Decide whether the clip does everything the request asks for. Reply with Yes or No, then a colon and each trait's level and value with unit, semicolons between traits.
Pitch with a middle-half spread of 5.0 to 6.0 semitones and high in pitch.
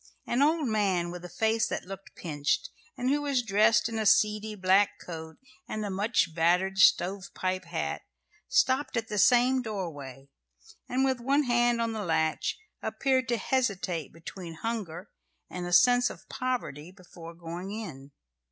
Yes: wide, 5.5 semitones; high, 205 Hz